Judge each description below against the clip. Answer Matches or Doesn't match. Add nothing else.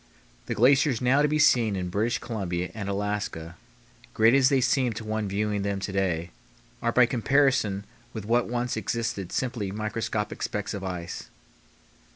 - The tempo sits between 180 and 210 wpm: Doesn't match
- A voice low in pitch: Matches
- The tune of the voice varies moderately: Matches